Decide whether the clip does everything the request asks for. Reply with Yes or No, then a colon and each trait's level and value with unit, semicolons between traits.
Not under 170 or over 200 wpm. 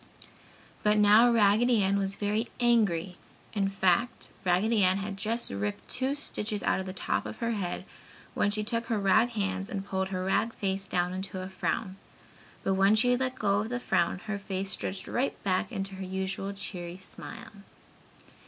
Yes: average, 180 wpm